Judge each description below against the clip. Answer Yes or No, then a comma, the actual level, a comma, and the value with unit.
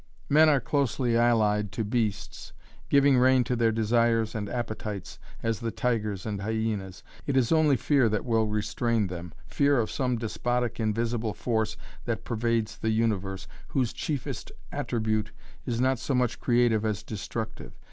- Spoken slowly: No, average, 155 wpm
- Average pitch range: No, narrow, 2.3 semitones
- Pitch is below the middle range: Yes, low, 115 Hz